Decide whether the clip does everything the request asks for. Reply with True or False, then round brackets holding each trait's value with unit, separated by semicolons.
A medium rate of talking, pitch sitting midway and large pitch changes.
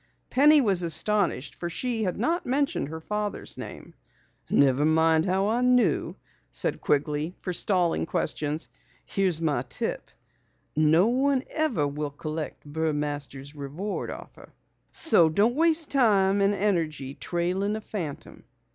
False (130 wpm; 180 Hz; 6.0 semitones)